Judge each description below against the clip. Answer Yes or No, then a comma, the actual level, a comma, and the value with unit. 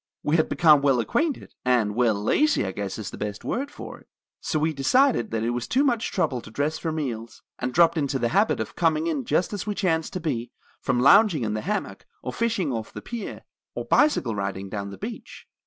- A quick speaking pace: Yes, fast, 225 wpm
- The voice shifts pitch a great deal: Yes, wide, 8.5 semitones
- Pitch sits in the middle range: Yes, medium, 145 Hz